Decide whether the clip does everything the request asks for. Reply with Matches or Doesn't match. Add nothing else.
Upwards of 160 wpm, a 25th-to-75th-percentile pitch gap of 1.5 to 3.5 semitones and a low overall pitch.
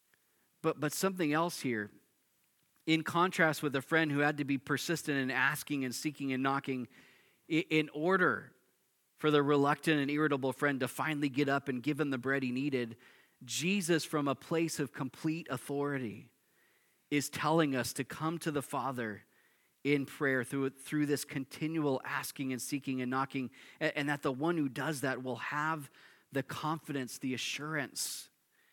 Doesn't match